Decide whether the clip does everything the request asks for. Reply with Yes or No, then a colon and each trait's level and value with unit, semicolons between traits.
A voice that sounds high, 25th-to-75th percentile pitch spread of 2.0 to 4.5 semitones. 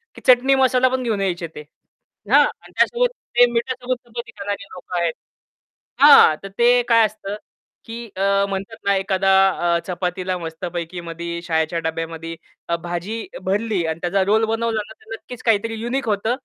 No: high, 200 Hz; average, 5.1 semitones